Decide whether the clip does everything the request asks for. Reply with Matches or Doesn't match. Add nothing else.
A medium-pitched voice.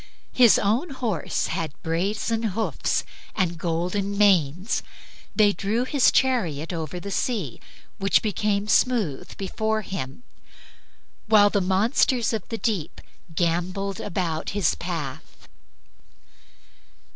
Doesn't match